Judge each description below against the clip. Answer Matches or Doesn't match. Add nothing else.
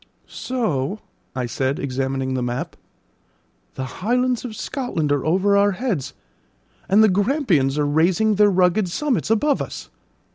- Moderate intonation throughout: Doesn't match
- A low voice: Doesn't match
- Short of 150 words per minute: Matches